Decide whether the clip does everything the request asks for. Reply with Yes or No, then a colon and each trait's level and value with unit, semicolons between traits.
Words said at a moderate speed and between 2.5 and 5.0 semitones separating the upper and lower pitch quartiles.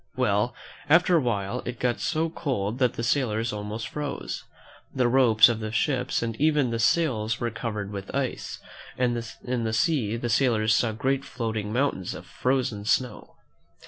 Yes: average, 170 wpm; average, 3.3 semitones